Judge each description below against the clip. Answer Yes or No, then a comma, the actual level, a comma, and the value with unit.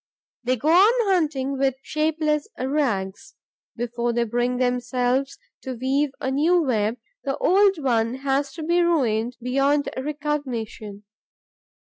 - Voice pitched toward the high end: Yes, very high, 265 Hz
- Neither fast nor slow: No, slow, 125 wpm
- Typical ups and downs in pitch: Yes, average, 3.7 semitones